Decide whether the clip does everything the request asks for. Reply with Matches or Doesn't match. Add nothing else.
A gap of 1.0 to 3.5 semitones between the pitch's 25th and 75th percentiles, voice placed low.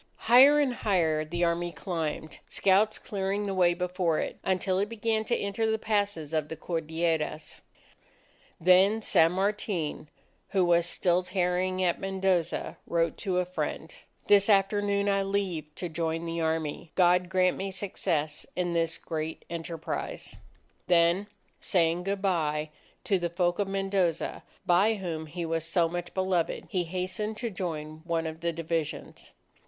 Doesn't match